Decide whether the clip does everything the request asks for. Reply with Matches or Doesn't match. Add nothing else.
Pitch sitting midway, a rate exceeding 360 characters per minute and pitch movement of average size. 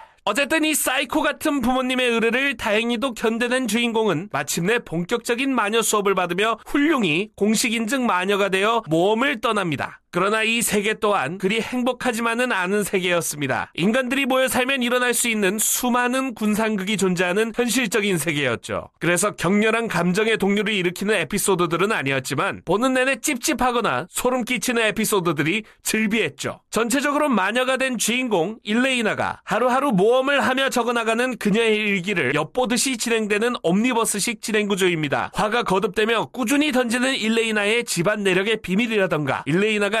Doesn't match